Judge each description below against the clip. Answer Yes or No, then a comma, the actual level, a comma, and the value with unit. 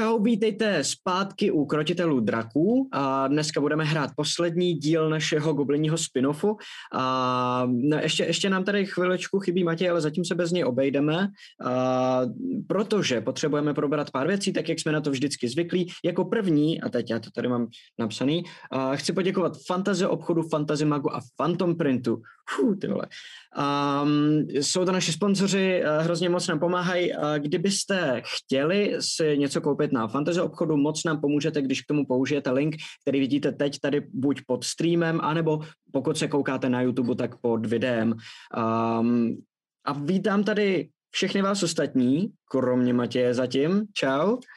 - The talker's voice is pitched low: No, medium, 150 Hz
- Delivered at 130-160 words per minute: Yes, average, 155 wpm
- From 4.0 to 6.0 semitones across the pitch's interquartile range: Yes, average, 4.9 semitones